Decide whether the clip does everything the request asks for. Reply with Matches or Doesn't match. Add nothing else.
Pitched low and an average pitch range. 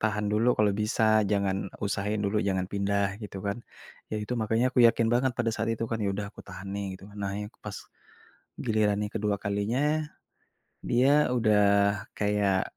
Doesn't match